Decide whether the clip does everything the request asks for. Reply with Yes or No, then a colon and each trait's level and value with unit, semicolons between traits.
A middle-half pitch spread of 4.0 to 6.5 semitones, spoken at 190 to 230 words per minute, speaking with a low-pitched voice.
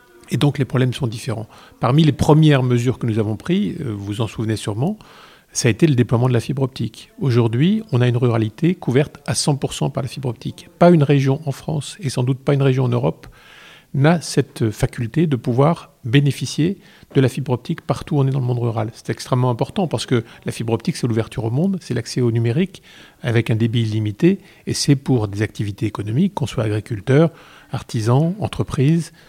Yes: average, 4.6 semitones; average, 210 wpm; low, 130 Hz